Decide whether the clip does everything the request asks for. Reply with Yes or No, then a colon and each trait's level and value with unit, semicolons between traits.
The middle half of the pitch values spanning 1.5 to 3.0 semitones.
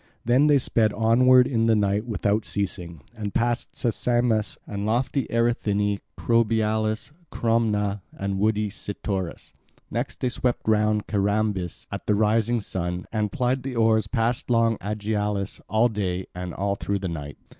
Yes: narrow, 2.4 semitones